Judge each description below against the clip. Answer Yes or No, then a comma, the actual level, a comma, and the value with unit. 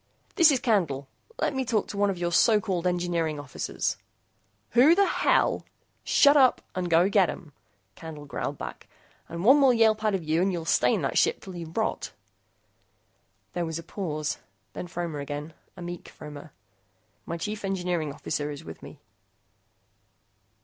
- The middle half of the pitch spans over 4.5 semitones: Yes, average, 4.9 semitones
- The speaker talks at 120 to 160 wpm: No, average, 175 wpm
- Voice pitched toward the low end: No, medium, 175 Hz